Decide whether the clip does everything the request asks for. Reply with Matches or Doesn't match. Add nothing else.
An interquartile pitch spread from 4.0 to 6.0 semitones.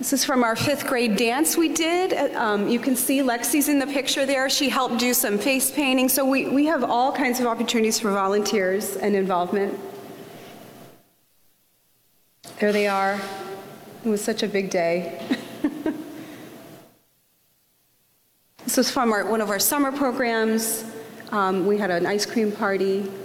Matches